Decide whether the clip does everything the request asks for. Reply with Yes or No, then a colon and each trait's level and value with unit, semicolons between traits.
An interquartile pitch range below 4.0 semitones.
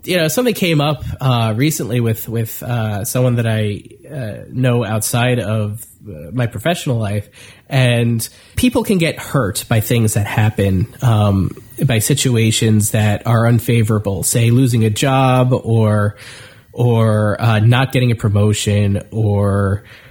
Yes: average, 3.0 semitones